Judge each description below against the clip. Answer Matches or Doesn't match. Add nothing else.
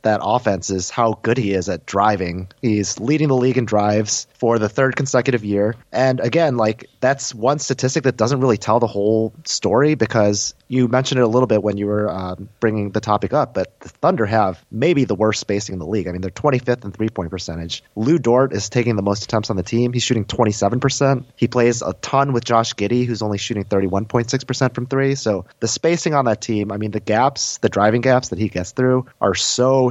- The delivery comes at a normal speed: Doesn't match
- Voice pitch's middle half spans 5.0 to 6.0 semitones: Doesn't match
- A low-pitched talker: Matches